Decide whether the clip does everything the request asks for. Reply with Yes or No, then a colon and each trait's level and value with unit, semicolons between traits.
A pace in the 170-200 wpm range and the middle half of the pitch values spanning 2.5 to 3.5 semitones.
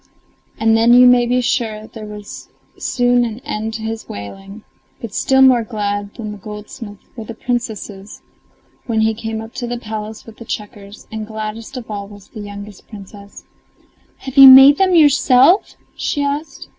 Yes: average, 175 wpm; average, 2.8 semitones